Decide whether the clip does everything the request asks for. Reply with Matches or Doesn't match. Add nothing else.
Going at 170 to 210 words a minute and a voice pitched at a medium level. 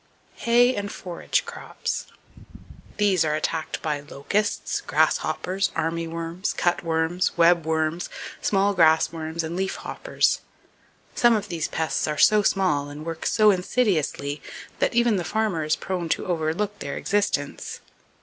Doesn't match